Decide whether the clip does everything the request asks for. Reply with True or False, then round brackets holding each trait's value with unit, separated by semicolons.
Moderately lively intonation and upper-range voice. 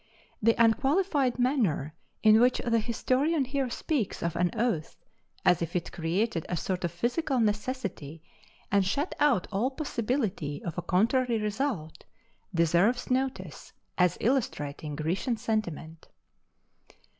False (6.6 semitones; 220 Hz)